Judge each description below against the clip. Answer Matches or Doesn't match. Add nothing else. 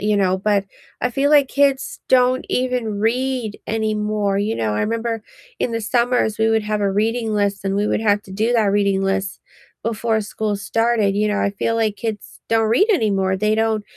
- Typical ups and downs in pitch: Doesn't match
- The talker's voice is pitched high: Matches